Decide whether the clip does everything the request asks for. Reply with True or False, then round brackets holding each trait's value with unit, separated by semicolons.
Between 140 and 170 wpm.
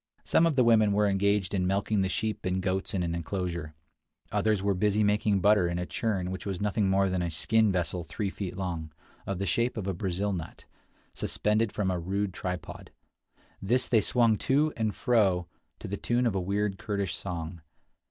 False (200 wpm)